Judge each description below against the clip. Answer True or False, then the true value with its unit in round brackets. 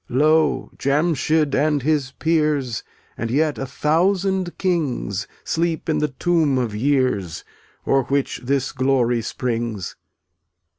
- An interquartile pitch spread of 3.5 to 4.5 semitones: True (4.0 semitones)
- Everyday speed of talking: False (115 wpm)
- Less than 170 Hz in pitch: True (140 Hz)